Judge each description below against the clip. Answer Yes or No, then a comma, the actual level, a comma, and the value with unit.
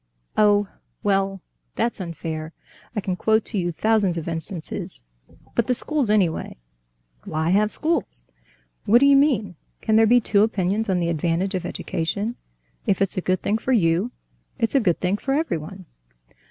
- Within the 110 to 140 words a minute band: No, average, 165 wpm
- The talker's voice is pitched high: Yes, high, 195 Hz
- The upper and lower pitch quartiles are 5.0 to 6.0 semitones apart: No, average, 4.3 semitones